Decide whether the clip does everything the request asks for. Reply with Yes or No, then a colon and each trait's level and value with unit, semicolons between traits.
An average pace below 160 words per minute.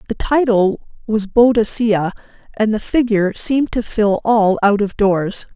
Yes: average, 150 wpm